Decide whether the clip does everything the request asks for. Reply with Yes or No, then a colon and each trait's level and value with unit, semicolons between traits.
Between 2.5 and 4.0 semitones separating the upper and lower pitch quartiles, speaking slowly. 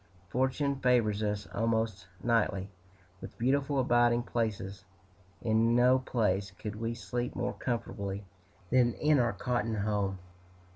Yes: average, 3.2 semitones; slow, 125 wpm